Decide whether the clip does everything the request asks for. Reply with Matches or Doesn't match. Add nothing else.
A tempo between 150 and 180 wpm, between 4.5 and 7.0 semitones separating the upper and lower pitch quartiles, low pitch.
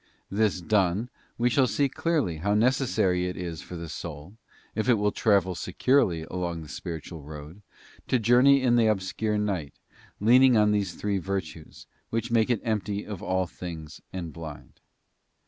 Matches